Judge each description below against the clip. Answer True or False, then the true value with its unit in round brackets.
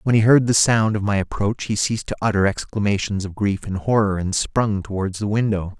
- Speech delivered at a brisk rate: True (230 wpm)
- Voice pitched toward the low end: True (105 Hz)